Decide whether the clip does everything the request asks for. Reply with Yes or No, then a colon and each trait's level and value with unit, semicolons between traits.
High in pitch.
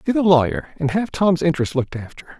No: medium, 155 Hz